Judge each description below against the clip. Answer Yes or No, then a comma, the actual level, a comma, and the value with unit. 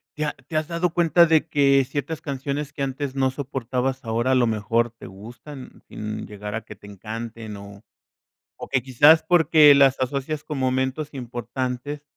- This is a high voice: No, low, 130 Hz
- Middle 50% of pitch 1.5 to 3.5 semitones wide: No, average, 4.1 semitones